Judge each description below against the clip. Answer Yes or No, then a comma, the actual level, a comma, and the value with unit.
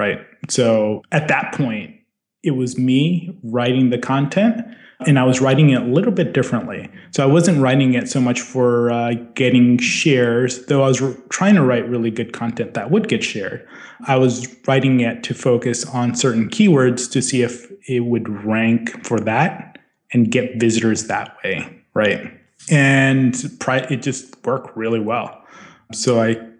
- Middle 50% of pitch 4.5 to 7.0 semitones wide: No, narrow, 2.5 semitones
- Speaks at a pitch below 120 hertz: No, low, 125 Hz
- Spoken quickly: No, average, 175 wpm